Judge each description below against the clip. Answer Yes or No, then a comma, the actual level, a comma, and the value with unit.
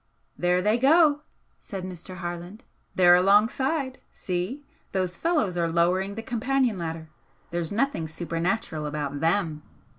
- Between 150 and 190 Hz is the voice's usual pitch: Yes, medium, 185 Hz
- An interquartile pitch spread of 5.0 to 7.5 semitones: Yes, wide, 5.5 semitones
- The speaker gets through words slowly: Yes, slow, 125 wpm